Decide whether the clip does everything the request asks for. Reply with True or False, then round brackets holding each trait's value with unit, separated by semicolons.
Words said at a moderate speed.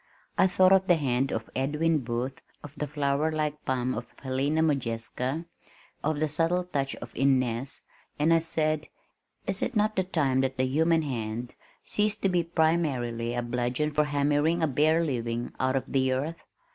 True (170 wpm)